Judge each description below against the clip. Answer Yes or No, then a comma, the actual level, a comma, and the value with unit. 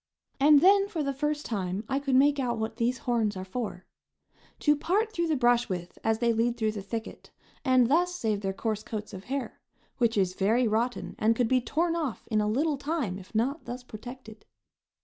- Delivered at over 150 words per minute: Yes, fast, 205 wpm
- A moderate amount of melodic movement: Yes, average, 4.6 semitones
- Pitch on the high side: Yes, high, 240 Hz